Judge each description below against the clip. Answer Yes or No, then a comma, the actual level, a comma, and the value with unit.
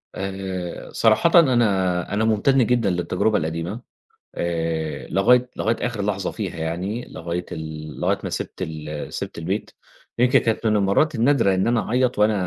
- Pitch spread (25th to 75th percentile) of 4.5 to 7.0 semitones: Yes, average, 5.1 semitones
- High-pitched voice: No, low, 100 Hz